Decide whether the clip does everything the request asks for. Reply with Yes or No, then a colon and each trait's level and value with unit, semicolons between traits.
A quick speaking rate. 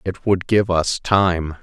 No: average, 185 wpm